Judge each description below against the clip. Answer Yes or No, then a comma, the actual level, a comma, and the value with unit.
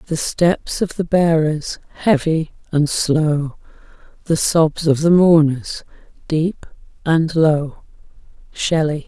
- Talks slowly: Yes, slow, 110 wpm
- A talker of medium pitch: Yes, medium, 160 Hz